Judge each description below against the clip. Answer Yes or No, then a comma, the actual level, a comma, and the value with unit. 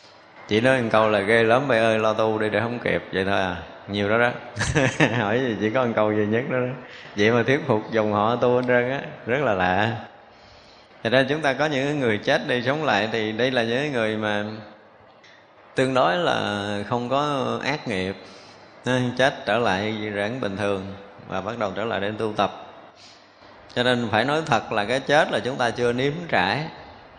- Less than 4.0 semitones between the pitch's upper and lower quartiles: Yes, average, 3.3 semitones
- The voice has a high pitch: No, low, 115 Hz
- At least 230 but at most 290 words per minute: No, average, 215 wpm